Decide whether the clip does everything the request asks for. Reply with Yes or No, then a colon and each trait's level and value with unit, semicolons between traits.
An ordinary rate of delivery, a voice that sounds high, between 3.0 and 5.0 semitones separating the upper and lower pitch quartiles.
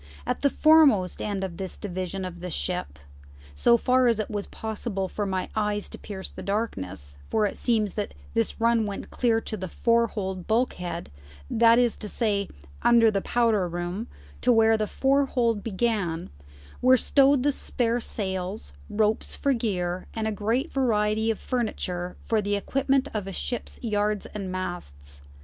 Yes: average, 170 wpm; high, 210 Hz; average, 3.7 semitones